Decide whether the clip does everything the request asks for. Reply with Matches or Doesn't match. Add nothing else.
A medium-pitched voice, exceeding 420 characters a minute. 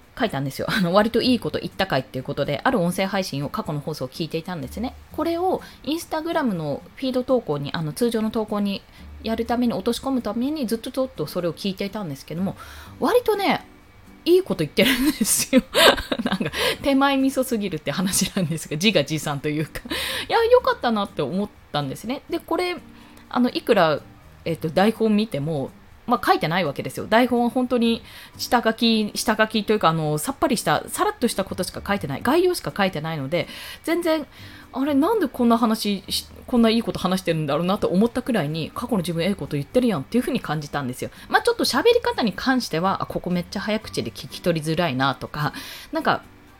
Doesn't match